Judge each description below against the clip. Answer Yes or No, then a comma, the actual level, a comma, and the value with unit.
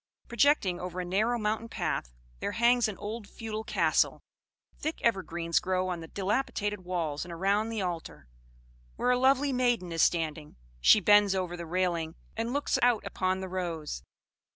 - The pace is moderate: Yes, average, 165 wpm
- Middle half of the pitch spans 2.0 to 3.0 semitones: No, average, 4.6 semitones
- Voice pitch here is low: No, high, 190 Hz